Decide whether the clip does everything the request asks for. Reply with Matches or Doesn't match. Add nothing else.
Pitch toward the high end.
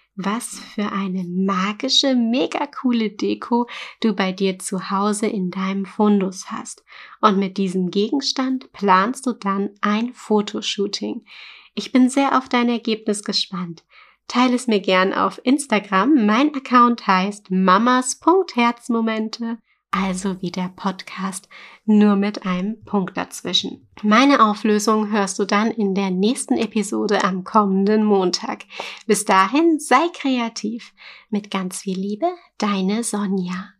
Matches